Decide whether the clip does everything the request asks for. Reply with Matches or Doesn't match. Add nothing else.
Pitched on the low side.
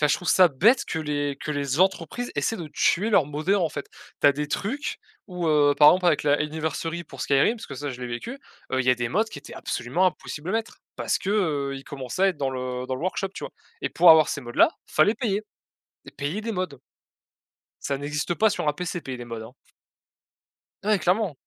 Doesn't match